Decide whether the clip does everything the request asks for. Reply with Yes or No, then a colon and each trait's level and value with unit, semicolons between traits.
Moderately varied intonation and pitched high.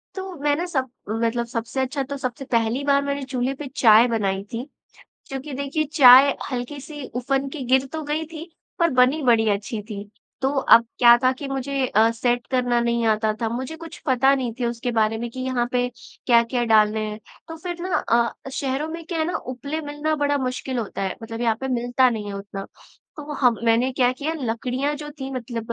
Yes: average, 3.3 semitones; very high, 255 Hz